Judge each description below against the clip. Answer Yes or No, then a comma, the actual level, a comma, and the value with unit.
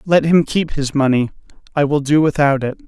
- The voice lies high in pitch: No, medium, 145 Hz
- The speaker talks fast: Yes, fast, 210 wpm